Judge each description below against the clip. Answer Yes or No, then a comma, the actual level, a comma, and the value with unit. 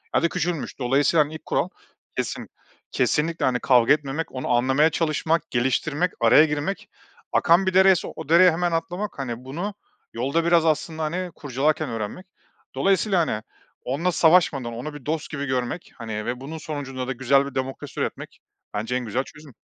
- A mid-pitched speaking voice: Yes, medium, 150 Hz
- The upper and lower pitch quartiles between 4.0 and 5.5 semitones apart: Yes, average, 4.4 semitones